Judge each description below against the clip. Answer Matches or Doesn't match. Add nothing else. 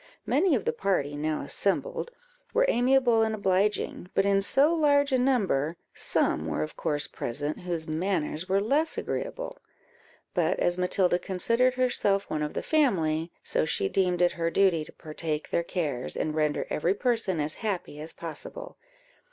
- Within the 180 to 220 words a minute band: Doesn't match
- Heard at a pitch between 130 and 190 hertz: Matches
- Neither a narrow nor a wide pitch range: Doesn't match